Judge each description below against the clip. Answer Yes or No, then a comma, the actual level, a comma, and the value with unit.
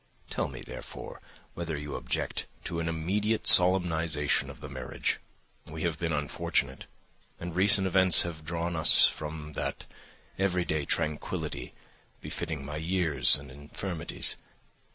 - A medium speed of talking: No, slow, 130 wpm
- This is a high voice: No, very low, 80 Hz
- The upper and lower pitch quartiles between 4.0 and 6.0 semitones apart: No, average, 2.9 semitones